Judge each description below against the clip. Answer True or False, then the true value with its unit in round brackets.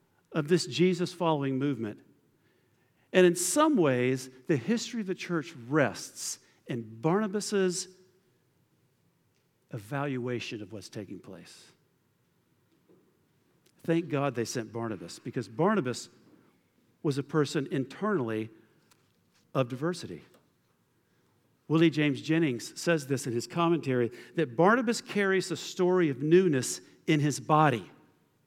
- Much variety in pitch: True (5.9 semitones)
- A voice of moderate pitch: True (150 Hz)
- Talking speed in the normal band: False (110 wpm)